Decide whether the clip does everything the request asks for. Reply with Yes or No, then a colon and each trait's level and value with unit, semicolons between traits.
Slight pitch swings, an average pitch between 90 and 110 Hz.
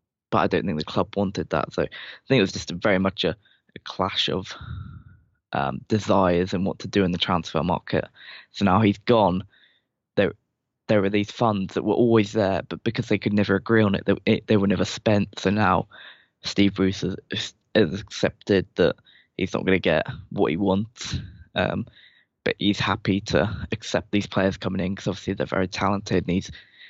Yes: narrow, 2.0 semitones; low, 100 Hz